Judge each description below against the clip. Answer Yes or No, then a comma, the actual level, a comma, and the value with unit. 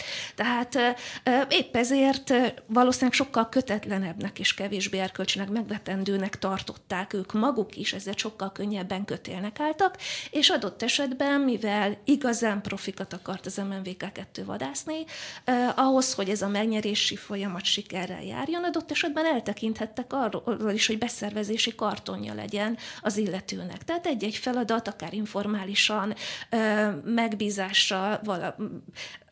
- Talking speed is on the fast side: No, average, 115 wpm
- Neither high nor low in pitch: No, high, 215 Hz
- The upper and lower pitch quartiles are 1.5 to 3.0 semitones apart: No, average, 4.0 semitones